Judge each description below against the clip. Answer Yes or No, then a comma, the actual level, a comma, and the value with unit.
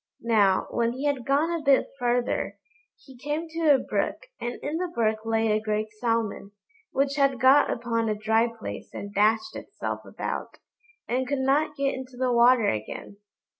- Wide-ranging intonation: No, average, 3.9 semitones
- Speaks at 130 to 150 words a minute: No, average, 175 wpm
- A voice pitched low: No, high, 245 Hz